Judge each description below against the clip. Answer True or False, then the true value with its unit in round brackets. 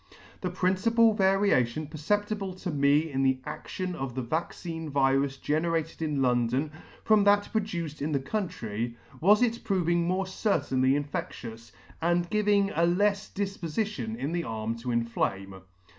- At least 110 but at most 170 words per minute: True (145 wpm)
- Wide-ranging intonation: True (6.6 semitones)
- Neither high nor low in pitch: True (165 Hz)